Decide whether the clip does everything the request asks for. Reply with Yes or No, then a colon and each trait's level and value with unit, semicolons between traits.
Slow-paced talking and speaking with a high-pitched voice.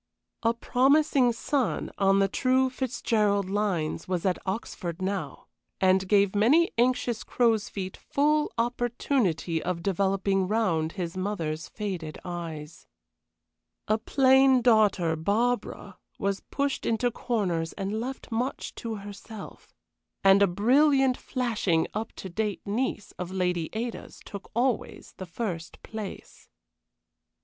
Yes: slow, 120 wpm; high, 205 Hz